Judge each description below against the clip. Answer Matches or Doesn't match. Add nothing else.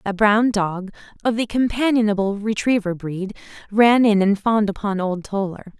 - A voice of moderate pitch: Doesn't match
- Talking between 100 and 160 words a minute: Matches